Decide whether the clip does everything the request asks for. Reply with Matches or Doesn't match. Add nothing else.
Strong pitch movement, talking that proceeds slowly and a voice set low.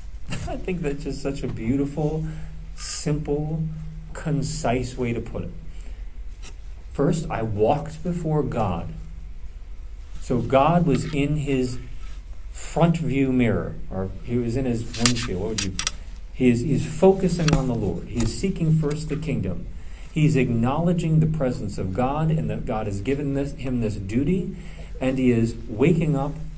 Doesn't match